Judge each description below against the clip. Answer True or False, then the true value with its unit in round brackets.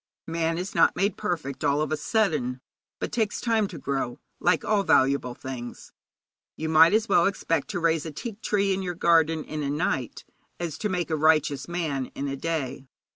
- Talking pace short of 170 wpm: False (195 wpm)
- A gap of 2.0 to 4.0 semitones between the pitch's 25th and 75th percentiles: False (4.5 semitones)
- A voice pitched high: False (160 Hz)